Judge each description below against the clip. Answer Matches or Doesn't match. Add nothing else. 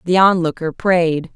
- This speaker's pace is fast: Doesn't match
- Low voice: Doesn't match